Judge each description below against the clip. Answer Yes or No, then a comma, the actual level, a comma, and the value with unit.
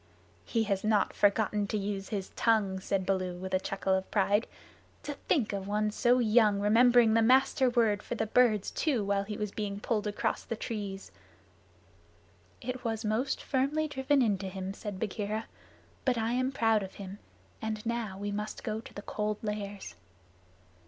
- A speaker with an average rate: Yes, average, 170 wpm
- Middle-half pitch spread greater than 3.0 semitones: No, narrow, 2.6 semitones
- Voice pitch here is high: Yes, high, 210 Hz